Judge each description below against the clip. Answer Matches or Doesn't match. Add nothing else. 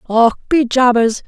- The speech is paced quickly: Doesn't match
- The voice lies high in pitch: Matches